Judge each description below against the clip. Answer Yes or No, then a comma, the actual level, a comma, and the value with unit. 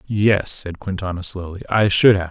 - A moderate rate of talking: Yes, average, 180 wpm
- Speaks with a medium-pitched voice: No, very low, 95 Hz